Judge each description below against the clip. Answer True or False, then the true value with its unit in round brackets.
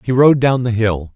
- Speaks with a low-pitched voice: True (115 Hz)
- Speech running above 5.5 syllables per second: False (4.8 syllables/s)